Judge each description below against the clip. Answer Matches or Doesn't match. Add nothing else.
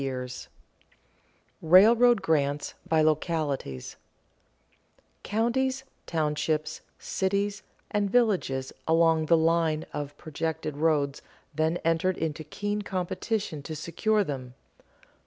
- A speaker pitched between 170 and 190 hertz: Doesn't match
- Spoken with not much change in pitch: Doesn't match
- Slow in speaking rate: Matches